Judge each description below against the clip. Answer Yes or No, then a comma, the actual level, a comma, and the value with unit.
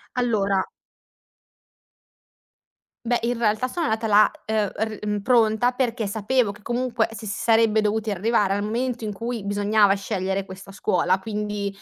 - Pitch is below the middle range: No, high, 215 Hz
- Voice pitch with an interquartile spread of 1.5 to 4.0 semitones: Yes, narrow, 2.5 semitones